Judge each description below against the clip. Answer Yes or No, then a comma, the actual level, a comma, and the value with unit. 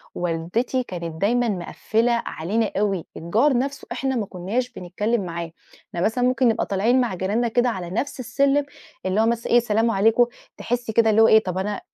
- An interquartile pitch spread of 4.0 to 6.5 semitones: Yes, average, 4.4 semitones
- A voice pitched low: No, high, 225 Hz